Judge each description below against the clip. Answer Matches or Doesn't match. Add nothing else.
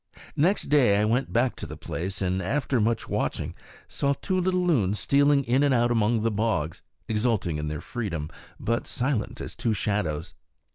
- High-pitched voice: Doesn't match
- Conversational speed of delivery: Matches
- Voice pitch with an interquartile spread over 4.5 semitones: Matches